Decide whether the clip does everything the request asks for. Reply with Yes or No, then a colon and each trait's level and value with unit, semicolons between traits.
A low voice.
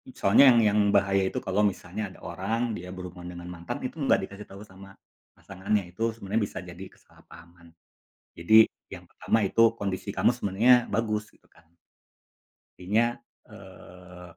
Yes: low, 100 Hz